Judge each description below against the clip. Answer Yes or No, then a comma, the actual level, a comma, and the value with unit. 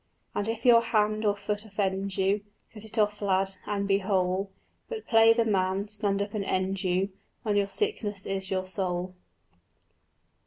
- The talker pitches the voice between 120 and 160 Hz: No, high, 200 Hz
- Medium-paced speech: Yes, average, 170 wpm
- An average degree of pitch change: No, narrow, 1.8 semitones